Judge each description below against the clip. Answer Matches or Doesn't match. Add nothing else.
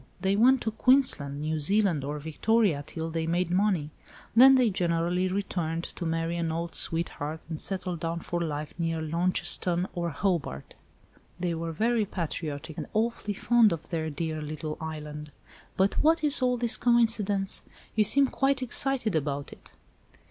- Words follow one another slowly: Doesn't match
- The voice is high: Doesn't match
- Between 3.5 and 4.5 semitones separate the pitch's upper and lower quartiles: Doesn't match